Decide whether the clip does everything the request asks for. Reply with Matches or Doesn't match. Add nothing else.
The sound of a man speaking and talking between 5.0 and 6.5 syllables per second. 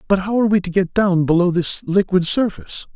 Matches